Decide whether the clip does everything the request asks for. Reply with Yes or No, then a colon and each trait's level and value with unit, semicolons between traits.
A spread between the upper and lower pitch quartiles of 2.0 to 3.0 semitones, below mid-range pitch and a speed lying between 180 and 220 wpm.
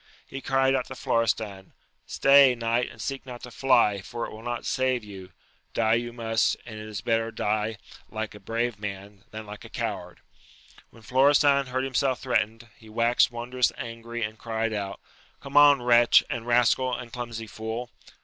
Yes: narrow, 2.4 semitones; low, 115 Hz; average, 185 wpm